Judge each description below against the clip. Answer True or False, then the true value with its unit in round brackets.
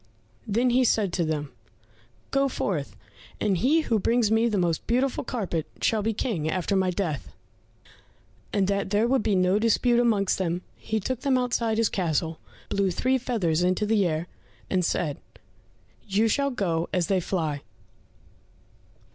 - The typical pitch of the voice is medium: False (200 Hz)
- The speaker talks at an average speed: True (160 wpm)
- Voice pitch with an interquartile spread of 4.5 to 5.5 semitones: True (4.9 semitones)